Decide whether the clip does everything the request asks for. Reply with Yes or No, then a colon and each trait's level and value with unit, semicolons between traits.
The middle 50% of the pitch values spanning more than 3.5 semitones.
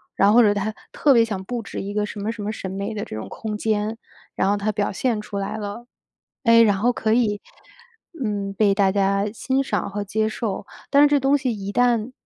No: narrow, 2.4 semitones